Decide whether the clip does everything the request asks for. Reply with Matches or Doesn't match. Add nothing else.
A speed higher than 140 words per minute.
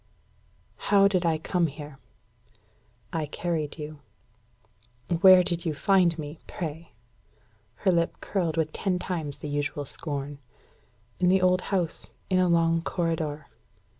Doesn't match